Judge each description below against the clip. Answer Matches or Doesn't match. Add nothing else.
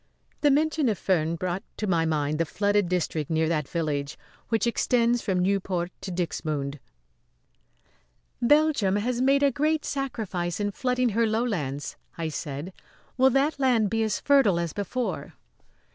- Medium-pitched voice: Doesn't match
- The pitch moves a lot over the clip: Matches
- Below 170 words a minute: Matches